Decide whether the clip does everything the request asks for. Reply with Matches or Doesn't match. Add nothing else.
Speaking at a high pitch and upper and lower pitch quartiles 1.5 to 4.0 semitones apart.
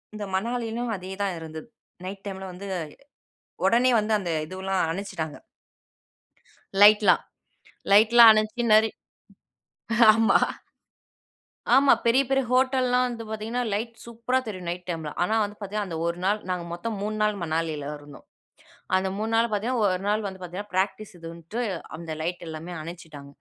Doesn't match